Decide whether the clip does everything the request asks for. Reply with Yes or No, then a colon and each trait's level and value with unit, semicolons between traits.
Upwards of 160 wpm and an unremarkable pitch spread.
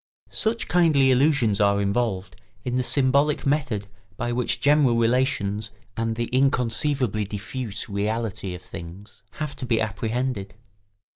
No: slow, 135 wpm; average, 4.5 semitones